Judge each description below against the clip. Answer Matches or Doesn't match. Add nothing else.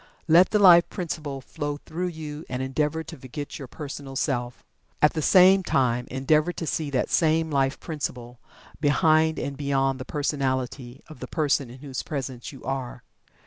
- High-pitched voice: Doesn't match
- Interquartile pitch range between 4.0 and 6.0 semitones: Doesn't match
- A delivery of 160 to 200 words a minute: Matches